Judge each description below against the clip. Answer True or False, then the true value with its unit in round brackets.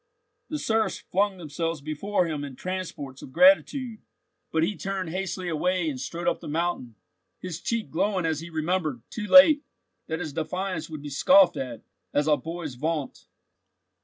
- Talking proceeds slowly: False (165 wpm)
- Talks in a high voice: False (170 Hz)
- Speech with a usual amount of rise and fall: True (3.9 semitones)